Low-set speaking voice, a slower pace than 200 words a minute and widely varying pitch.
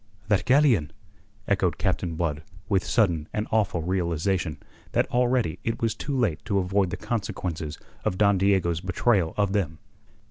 No: very low, 95 Hz; average, 150 wpm; average, 4.2 semitones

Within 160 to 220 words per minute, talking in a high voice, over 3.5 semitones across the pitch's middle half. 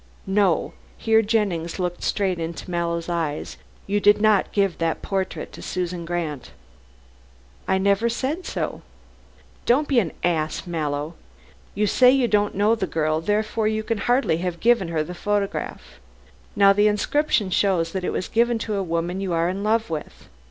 Yes: average, 170 wpm; high, 195 Hz; average, 4.0 semitones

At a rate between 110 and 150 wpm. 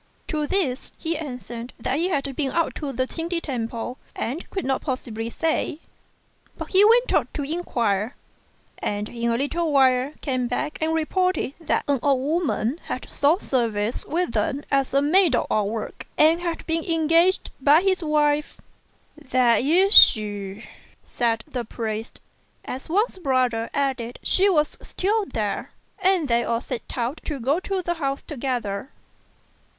No: average, 160 wpm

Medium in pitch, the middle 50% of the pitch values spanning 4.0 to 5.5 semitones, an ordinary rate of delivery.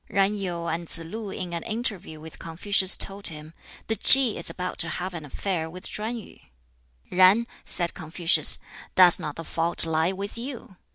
No: medium, 180 Hz; average, 3.6 semitones; average, 180 wpm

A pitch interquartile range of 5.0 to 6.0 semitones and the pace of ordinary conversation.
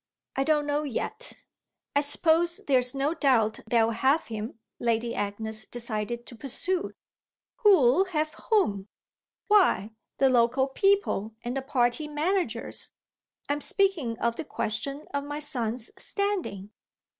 No: average, 5.3 semitones; slow, 130 wpm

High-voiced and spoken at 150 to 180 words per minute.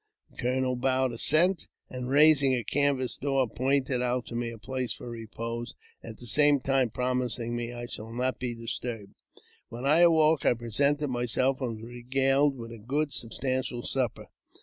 No: low, 125 Hz; average, 170 wpm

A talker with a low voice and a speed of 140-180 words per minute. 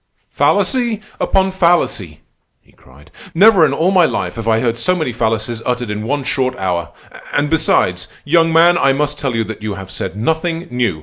No: low, 130 Hz; average, 190 wpm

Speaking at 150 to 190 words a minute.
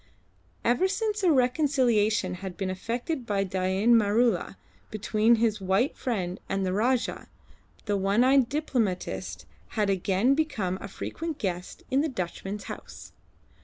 No: slow, 135 wpm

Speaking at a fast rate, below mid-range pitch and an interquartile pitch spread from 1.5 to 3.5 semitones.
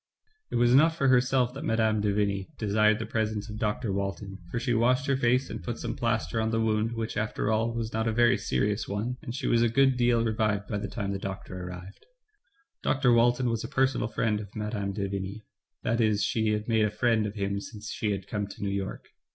Yes: fast, 235 wpm; low, 110 Hz; narrow, 2.6 semitones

